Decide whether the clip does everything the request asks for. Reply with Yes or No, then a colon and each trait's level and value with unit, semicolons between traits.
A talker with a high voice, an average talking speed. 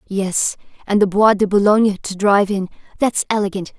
Yes: high, 200 Hz; average, 175 wpm